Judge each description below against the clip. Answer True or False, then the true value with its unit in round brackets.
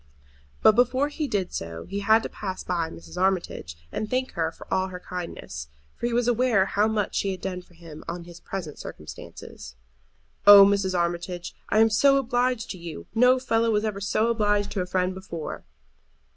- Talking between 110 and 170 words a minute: False (195 wpm)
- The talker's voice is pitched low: False (195 Hz)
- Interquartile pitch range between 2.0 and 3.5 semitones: False (4.3 semitones)